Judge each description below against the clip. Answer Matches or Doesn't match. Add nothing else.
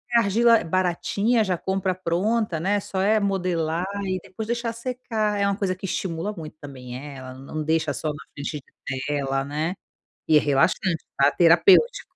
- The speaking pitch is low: Doesn't match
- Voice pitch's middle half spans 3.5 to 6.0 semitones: Matches